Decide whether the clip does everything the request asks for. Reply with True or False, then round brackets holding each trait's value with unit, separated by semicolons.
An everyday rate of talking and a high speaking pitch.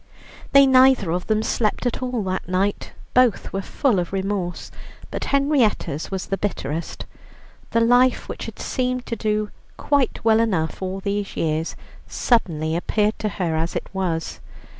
True (160 wpm; 205 Hz)